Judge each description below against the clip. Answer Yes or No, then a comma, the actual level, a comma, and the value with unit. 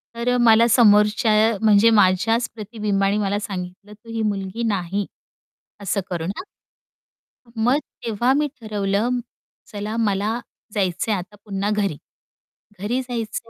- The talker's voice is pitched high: Yes, high, 210 Hz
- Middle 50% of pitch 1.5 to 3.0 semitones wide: Yes, narrow, 2.6 semitones